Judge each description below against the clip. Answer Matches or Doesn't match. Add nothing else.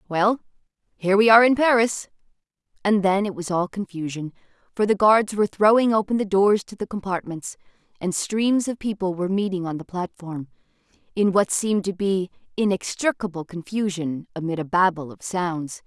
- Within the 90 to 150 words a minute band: Doesn't match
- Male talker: Doesn't match